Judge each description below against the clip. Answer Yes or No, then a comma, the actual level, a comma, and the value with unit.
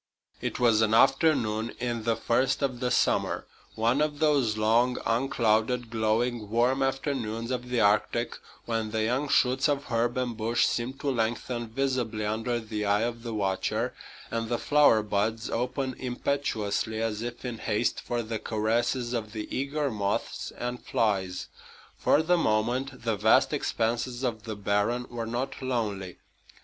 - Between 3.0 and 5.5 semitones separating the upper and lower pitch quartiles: No, narrow, 2.5 semitones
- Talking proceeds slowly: No, average, 160 wpm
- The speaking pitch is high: No, low, 120 Hz